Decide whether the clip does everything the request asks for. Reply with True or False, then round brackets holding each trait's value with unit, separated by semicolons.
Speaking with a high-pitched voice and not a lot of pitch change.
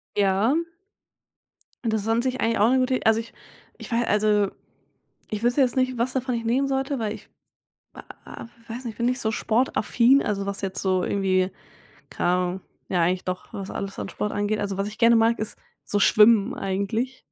False (220 Hz; 3.4 semitones)